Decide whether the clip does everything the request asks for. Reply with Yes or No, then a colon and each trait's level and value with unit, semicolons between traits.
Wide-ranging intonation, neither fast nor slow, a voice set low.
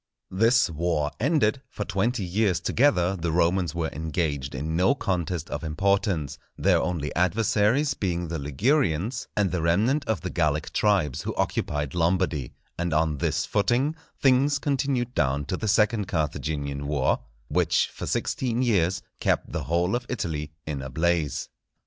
Yes: wide, 6.1 semitones; average, 155 wpm; very low, 90 Hz